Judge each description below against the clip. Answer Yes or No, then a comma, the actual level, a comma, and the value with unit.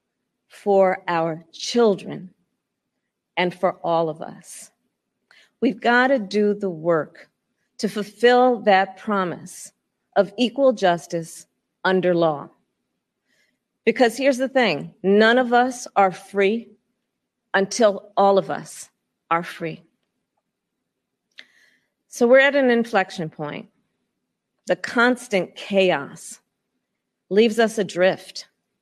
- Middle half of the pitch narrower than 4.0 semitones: No, average, 4.5 semitones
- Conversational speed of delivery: No, slow, 105 wpm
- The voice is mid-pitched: No, high, 200 Hz